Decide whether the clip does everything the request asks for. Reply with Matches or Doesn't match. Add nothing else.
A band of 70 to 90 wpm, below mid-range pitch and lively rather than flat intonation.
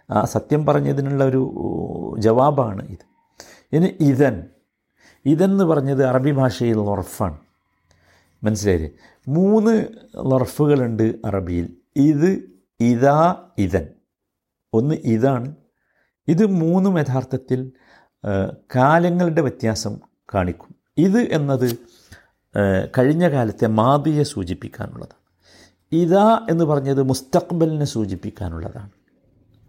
Matches